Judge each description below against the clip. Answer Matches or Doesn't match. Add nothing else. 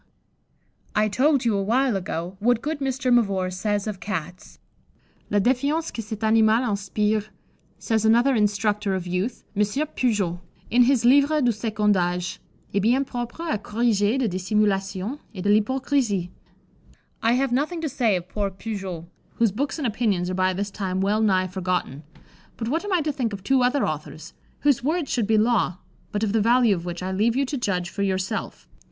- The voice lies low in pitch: Doesn't match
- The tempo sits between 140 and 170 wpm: Doesn't match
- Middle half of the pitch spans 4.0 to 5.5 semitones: Matches